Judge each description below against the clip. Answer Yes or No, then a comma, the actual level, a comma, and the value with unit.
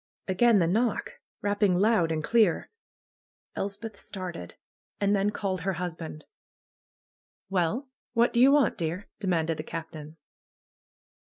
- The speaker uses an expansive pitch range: No, average, 4.4 semitones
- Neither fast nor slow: No, slow, 125 wpm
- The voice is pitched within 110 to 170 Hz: No, high, 190 Hz